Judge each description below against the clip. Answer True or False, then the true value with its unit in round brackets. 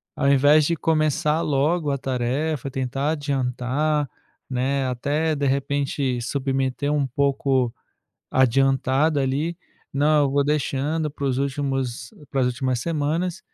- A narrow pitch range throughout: True (2.3 semitones)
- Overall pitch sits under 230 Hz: True (140 Hz)